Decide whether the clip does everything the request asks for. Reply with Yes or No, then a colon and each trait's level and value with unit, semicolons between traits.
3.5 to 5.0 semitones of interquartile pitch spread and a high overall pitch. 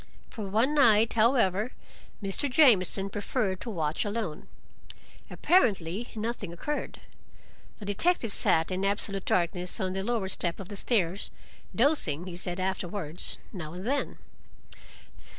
Yes: average, 4.2 semitones; high, 200 Hz